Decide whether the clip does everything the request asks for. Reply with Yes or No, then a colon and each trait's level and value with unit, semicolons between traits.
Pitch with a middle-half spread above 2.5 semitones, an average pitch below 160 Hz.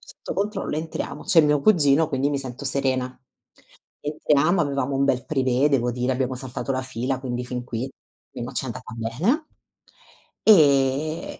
Yes: average, 2.9 semitones; low, 135 Hz